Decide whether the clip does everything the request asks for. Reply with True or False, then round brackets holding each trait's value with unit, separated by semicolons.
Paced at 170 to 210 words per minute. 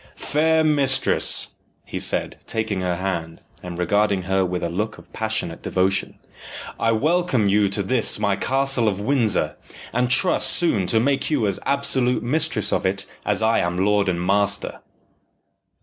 False (160 wpm)